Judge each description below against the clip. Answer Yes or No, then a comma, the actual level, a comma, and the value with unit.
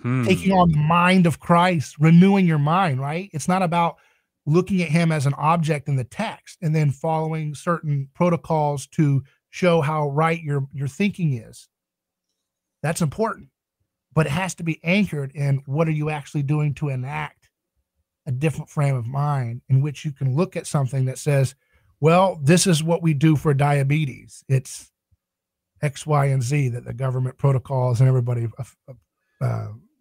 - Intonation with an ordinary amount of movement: Yes, average, 3.9 semitones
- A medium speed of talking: Yes, average, 170 wpm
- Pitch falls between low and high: Yes, medium, 150 Hz